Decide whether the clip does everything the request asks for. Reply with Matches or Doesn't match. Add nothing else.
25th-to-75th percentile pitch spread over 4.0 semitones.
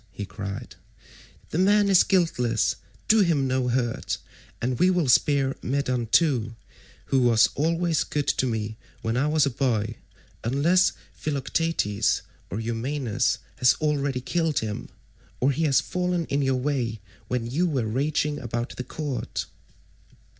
Matches